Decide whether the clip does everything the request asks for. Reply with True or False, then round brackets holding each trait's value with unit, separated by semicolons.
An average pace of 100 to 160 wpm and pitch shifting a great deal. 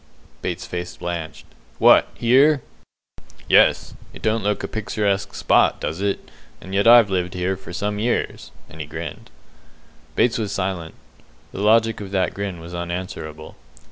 False (150 wpm; 3.3 semitones)